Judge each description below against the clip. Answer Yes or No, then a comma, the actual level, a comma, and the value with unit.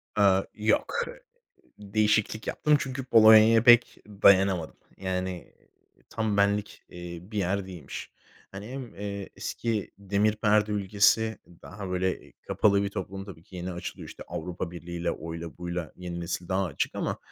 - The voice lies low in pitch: Yes, low, 100 Hz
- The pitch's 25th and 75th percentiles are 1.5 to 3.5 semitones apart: Yes, average, 2.9 semitones